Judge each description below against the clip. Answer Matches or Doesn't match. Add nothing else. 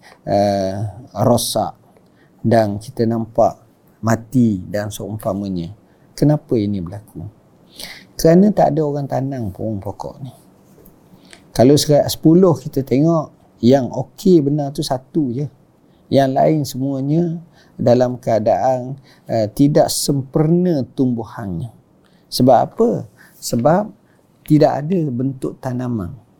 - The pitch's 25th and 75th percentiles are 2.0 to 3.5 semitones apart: Doesn't match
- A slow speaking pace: Doesn't match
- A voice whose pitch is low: Matches